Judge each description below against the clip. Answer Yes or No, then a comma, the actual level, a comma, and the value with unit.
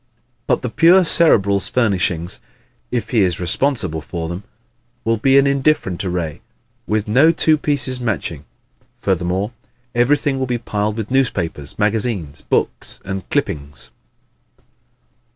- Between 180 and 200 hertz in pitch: No, low, 105 Hz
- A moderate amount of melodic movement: No, wide, 6.8 semitones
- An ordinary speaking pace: No, slow, 125 wpm